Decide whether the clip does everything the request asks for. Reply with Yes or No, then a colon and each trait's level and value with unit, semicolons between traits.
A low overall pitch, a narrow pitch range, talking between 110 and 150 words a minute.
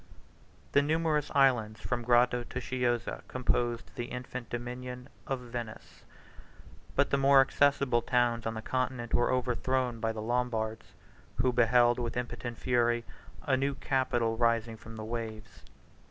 Yes: low, 120 Hz; narrow, 1.6 semitones; average, 140 wpm